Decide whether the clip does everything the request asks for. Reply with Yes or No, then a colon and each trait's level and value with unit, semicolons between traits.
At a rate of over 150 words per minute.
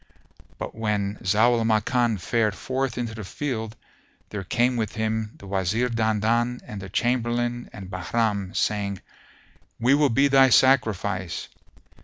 No: average, 140 wpm